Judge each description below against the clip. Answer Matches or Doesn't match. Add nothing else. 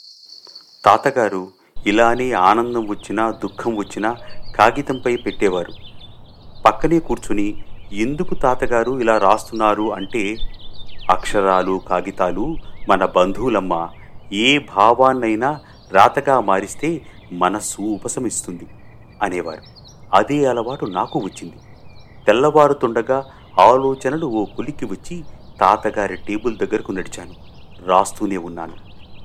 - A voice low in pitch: Matches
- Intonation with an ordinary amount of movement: Matches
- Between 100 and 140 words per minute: Doesn't match